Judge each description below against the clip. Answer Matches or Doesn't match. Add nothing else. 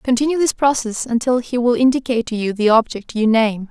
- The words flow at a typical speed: Doesn't match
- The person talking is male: Doesn't match